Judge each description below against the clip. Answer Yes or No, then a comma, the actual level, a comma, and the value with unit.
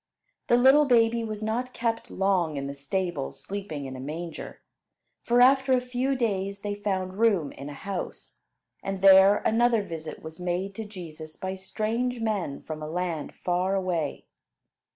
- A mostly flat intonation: No, average, 5.2 semitones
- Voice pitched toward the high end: Yes, high, 195 Hz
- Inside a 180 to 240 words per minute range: No, average, 165 wpm